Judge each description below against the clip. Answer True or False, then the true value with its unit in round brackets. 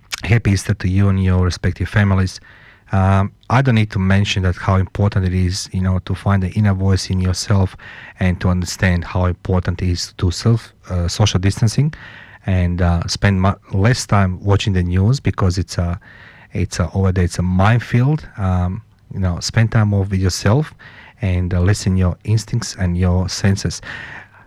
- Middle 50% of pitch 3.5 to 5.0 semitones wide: False (2.5 semitones)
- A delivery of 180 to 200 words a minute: True (185 wpm)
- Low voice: True (95 Hz)